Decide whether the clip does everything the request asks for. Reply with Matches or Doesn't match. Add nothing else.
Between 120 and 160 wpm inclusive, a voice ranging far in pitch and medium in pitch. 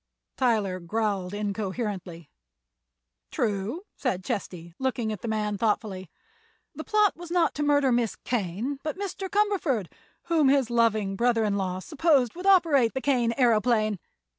Doesn't match